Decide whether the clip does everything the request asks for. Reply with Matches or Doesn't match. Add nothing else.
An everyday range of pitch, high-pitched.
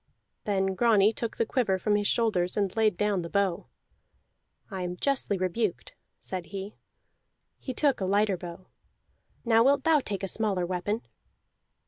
Matches